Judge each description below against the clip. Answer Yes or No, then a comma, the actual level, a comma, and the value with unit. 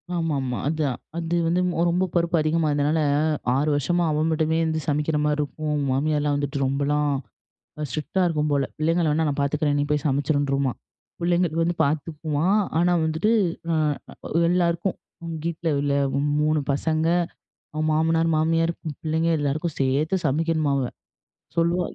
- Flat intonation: Yes, narrow, 2.3 semitones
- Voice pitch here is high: No, medium, 155 Hz